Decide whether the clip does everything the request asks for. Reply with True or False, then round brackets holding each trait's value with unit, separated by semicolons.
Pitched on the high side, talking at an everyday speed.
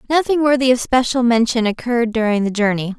True (240 Hz; 180 wpm)